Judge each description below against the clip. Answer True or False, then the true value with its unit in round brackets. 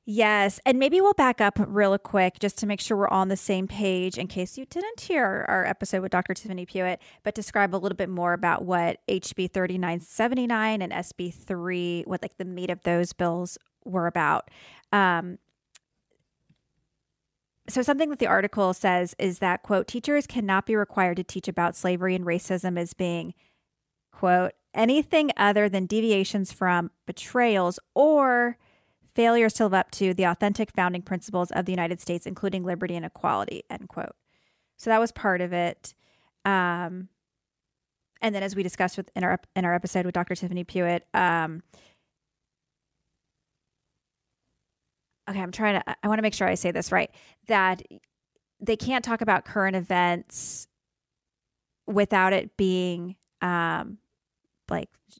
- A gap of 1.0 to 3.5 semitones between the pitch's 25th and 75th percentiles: True (2.8 semitones)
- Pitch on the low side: False (190 Hz)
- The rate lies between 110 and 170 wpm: True (160 wpm)